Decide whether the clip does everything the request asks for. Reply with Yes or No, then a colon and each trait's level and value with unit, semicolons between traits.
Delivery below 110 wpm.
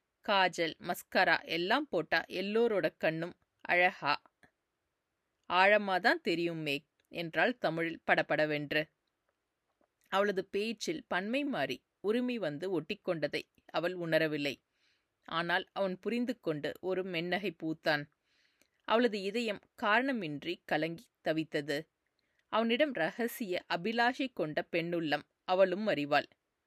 Yes: average, 90 wpm